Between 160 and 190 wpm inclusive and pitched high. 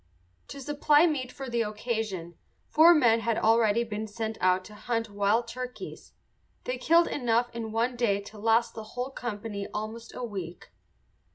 Yes: average, 165 wpm; high, 230 Hz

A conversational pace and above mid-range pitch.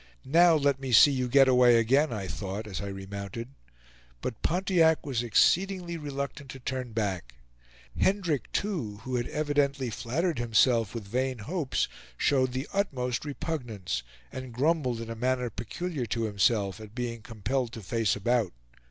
No: average, 155 wpm; low, 125 Hz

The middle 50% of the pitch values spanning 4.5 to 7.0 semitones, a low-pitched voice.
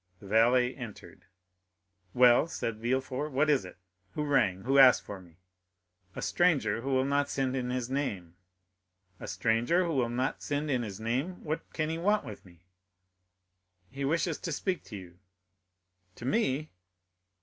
Yes: average, 4.8 semitones; low, 130 Hz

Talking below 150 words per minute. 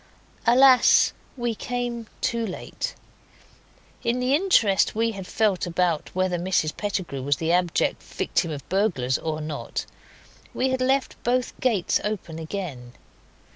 Yes: slow, 135 wpm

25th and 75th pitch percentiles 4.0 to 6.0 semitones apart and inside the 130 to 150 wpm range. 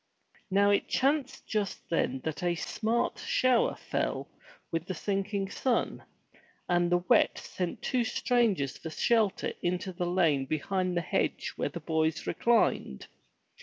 Yes: average, 4.5 semitones; average, 140 wpm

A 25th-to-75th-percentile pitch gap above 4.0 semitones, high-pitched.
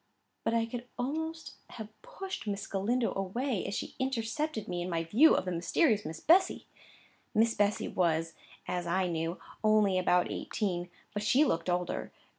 Yes: wide, 5.5 semitones; high, 205 Hz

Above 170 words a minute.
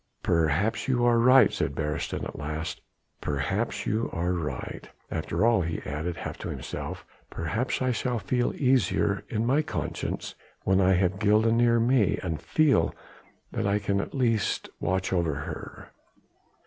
No: average, 155 wpm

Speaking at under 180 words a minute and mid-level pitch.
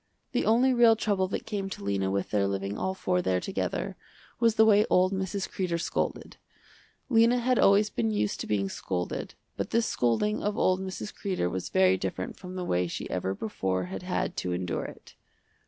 No: average, 195 wpm; medium, 180 Hz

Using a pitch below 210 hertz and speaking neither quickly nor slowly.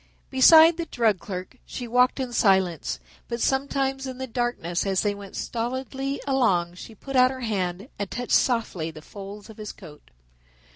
No: high, 235 Hz; average, 175 wpm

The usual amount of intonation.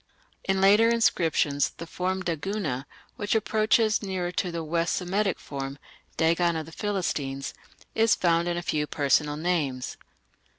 Yes: average, 4.4 semitones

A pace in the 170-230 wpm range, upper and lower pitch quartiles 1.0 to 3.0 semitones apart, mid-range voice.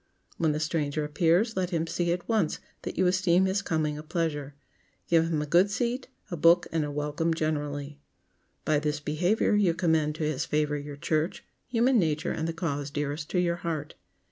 Yes: average, 195 wpm; average, 2.7 semitones; medium, 160 Hz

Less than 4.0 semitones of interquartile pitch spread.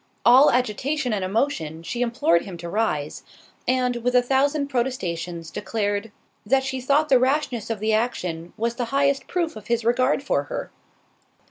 No: average, 4.6 semitones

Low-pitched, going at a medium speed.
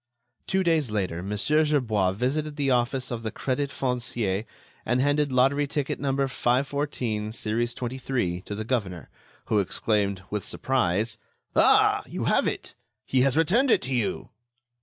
Yes: low, 125 Hz; average, 150 wpm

